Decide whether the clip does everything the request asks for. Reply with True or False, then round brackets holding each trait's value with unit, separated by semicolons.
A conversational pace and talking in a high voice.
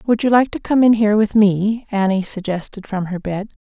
False (230 wpm; 205 Hz)